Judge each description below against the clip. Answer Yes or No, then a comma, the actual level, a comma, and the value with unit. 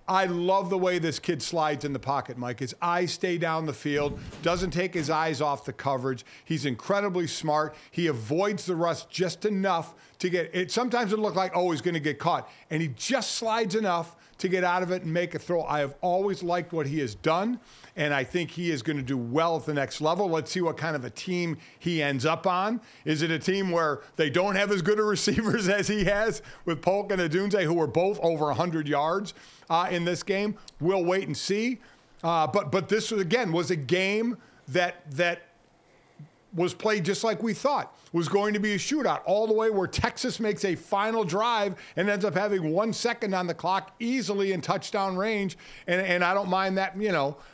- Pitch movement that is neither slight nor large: Yes, average, 4.0 semitones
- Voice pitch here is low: No, medium, 180 Hz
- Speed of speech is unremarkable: No, fast, 225 wpm